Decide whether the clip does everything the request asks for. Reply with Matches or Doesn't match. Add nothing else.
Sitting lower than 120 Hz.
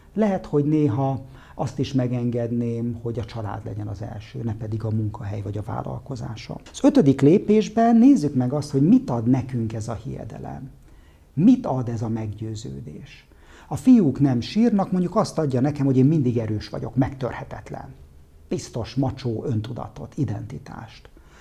Doesn't match